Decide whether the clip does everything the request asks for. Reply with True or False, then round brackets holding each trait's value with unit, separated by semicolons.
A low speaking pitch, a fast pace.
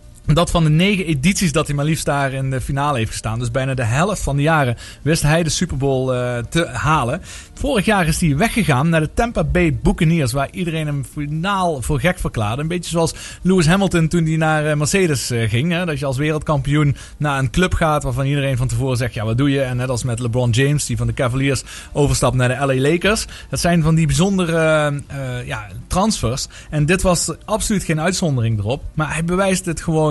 False (150 Hz; 220 wpm)